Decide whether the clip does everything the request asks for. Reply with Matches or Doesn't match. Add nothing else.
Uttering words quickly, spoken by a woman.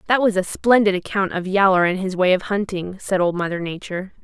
Matches